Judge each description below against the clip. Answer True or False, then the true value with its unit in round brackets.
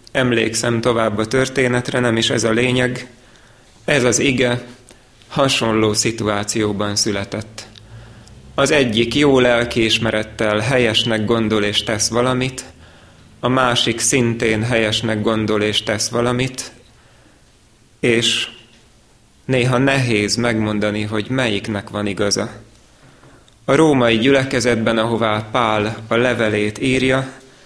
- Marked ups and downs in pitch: False (2.4 semitones)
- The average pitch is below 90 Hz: False (115 Hz)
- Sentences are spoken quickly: False (105 wpm)